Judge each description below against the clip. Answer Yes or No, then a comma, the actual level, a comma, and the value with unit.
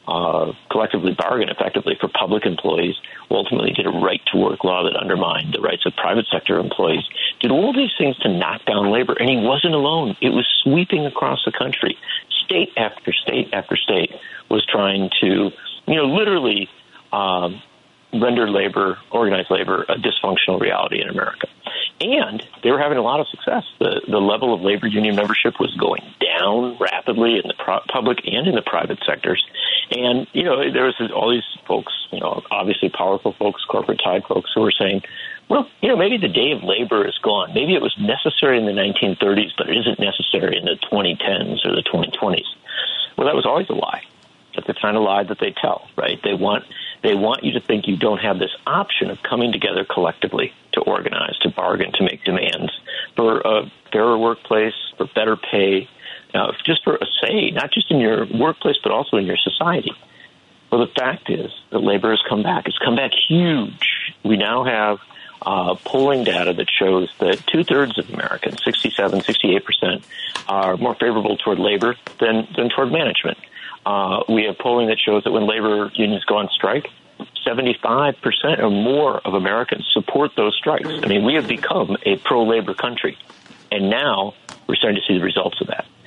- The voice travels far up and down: No, average, 3.4 semitones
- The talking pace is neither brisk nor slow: Yes, average, 190 wpm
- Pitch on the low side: Yes, low, 110 Hz